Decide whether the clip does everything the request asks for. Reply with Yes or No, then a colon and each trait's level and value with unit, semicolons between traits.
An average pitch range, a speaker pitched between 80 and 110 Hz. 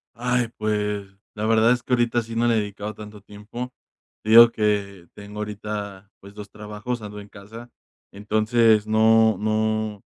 No: narrow, 1.5 semitones; low, 105 Hz